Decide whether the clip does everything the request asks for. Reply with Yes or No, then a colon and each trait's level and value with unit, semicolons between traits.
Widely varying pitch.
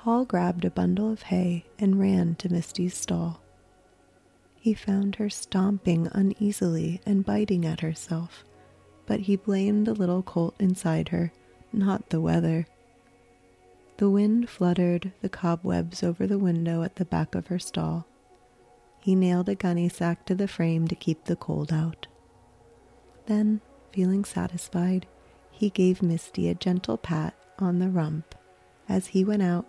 No: average, 3.9 semitones